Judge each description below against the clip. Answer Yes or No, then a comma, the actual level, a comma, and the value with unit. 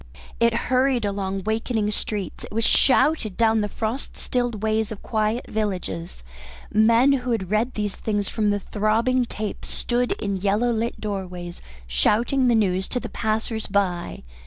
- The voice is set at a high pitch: Yes, high, 215 Hz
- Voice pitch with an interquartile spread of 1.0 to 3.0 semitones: Yes, narrow, 2.6 semitones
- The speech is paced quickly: No, average, 160 wpm